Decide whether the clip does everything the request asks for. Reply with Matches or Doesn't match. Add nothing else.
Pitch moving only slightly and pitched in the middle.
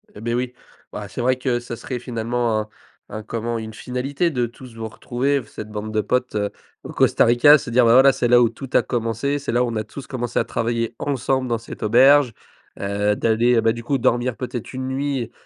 Doesn't match